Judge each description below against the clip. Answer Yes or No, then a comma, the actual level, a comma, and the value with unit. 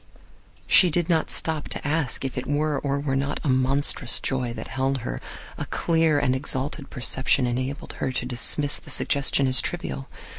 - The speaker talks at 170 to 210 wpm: Yes, average, 180 wpm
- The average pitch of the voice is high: No, low, 135 Hz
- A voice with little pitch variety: Yes, narrow, 2.3 semitones